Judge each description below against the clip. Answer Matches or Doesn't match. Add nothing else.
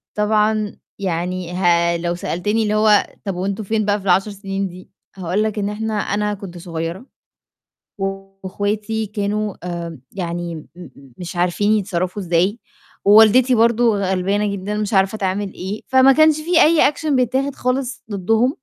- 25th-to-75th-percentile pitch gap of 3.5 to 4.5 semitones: Doesn't match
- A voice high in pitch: Matches